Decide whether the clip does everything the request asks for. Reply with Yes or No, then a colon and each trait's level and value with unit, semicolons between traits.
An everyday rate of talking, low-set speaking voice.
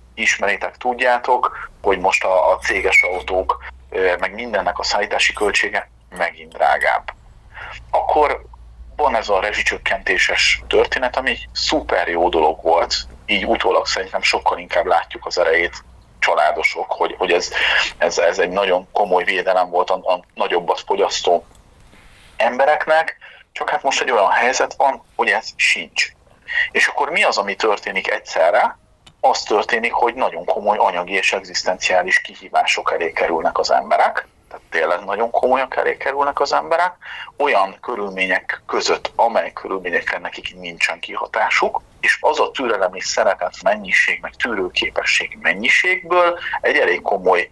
No: average, 140 wpm; medium, 180 Hz